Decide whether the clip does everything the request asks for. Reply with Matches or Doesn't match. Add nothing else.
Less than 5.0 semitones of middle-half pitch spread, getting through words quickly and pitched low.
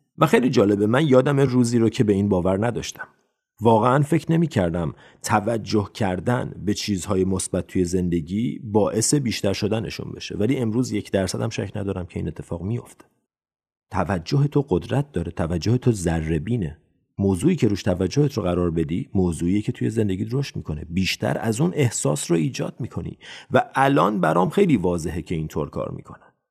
Doesn't match